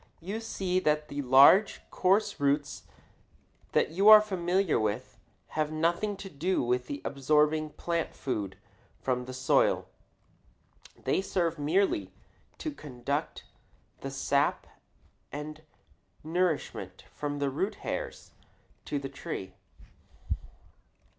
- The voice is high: No, medium, 155 Hz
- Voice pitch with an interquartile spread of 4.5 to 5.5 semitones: Yes, average, 5.1 semitones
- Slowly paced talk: Yes, slow, 110 wpm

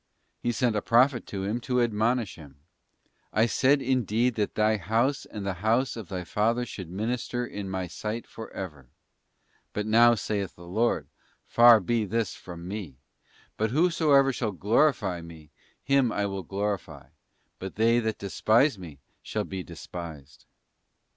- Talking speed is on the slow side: No, average, 160 wpm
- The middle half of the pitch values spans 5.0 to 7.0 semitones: No, average, 4.0 semitones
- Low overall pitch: Yes, low, 110 Hz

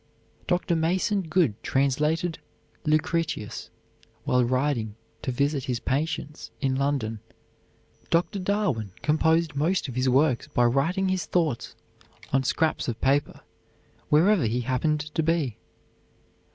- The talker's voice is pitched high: No, medium, 150 Hz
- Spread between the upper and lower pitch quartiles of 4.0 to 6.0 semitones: Yes, average, 4.4 semitones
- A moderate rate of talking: No, slow, 120 wpm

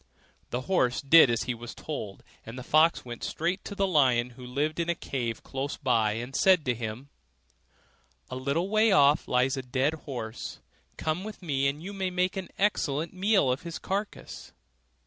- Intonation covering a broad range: Yes, wide, 6.1 semitones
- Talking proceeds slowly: No, average, 185 wpm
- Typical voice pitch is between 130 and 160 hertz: Yes, medium, 140 Hz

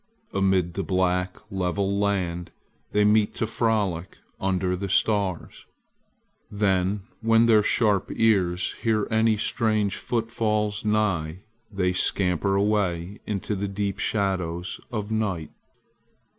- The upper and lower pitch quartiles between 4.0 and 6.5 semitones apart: No, average, 2.7 semitones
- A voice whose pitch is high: No, low, 100 Hz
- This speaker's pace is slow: Yes, slow, 115 wpm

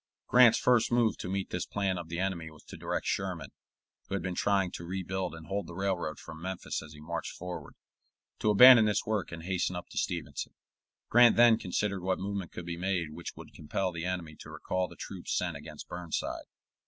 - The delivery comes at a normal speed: No, fast, 210 wpm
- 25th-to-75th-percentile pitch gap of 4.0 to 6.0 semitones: No, narrow, 2.6 semitones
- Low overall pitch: Yes, very low, 95 Hz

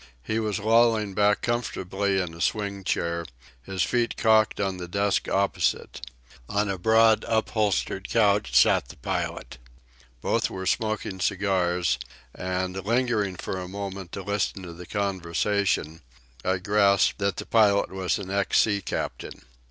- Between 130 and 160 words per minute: Yes, average, 145 wpm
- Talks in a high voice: No, low, 100 Hz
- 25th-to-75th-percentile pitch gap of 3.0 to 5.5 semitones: No, narrow, 2.4 semitones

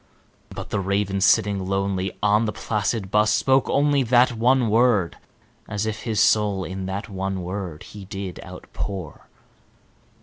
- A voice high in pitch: No, low, 100 Hz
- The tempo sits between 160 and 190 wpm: No, average, 145 wpm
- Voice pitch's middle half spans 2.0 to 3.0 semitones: Yes, narrow, 2.4 semitones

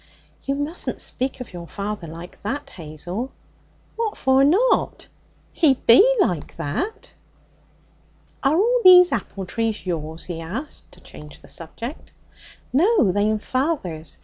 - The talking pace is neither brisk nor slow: No, slow, 130 wpm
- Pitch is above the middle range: Yes, high, 230 Hz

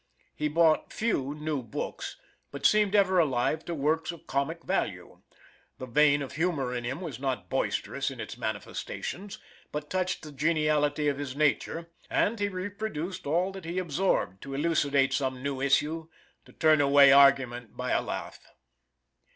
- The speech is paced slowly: No, average, 160 wpm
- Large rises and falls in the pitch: No, average, 3.6 semitones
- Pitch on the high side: No, medium, 150 Hz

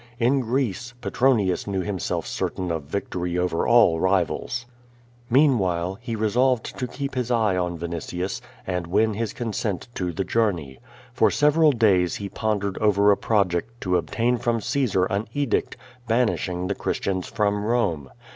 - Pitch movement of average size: Yes, average, 4.7 semitones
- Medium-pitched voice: No, low, 100 Hz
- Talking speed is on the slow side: No, average, 155 wpm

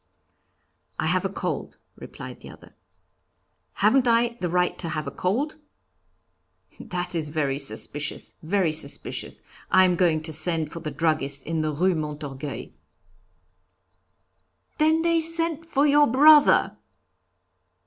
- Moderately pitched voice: Yes, medium, 175 Hz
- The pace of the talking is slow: Yes, slow, 130 wpm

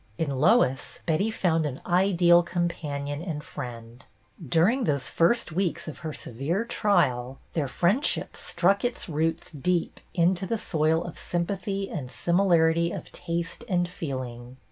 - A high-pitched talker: No, medium, 170 Hz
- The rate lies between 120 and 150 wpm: Yes, average, 140 wpm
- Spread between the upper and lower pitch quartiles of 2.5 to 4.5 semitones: Yes, average, 4.0 semitones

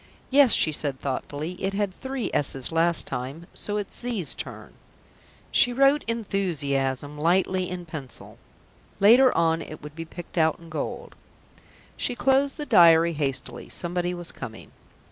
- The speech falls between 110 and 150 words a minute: Yes, average, 145 wpm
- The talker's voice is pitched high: No, medium, 170 Hz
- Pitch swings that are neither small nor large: No, wide, 5.7 semitones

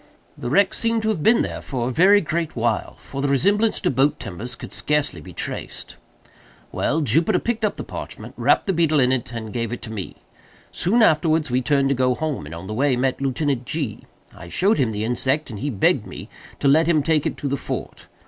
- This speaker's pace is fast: Yes, fast, 225 wpm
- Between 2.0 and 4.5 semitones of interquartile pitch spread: No, average, 5.1 semitones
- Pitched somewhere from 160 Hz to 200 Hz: No, medium, 140 Hz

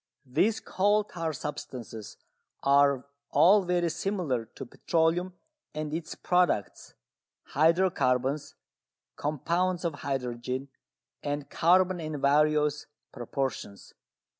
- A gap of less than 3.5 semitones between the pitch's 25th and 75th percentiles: No, average, 4.6 semitones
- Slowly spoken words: Yes, slow, 95 wpm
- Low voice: No, medium, 150 Hz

